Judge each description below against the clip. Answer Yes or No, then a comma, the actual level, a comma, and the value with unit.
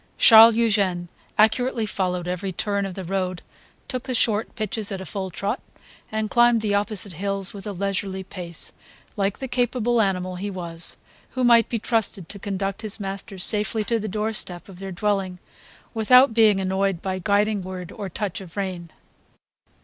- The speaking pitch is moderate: No, high, 200 Hz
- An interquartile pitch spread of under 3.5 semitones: Yes, average, 2.7 semitones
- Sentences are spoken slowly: No, average, 175 wpm